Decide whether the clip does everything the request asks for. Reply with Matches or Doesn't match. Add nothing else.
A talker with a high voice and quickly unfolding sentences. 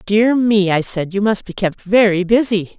Matches